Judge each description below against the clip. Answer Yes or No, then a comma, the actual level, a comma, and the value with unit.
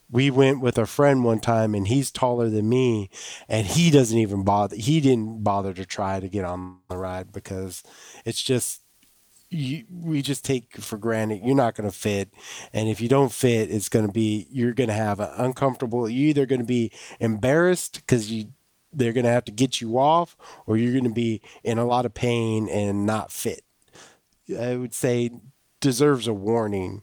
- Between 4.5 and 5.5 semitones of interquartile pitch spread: No, average, 3.6 semitones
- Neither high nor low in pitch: No, low, 115 Hz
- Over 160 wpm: Yes, average, 200 wpm